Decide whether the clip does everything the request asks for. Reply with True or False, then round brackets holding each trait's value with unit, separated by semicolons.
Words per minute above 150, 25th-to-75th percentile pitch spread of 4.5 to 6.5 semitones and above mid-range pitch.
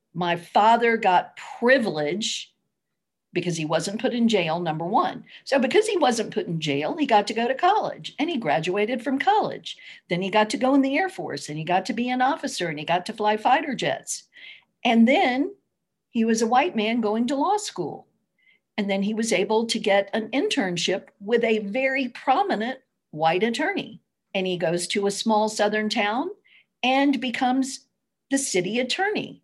True (190 wpm; 5.1 semitones; 225 Hz)